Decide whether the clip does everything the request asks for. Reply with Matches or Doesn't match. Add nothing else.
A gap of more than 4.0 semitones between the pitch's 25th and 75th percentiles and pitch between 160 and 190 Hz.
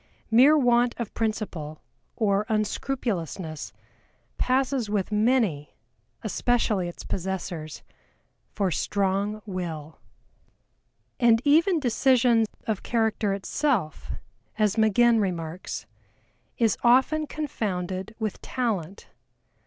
Doesn't match